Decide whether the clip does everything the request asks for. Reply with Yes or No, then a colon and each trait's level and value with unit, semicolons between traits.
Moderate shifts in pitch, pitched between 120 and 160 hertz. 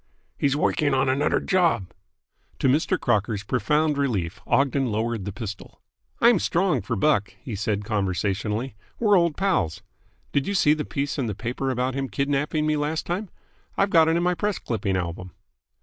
No: wide, 6.8 semitones; low, 135 Hz